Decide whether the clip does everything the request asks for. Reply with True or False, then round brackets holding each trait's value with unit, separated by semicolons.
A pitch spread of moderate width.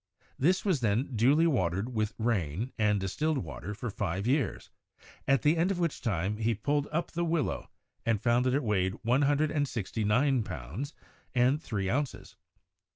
False (5.9 semitones)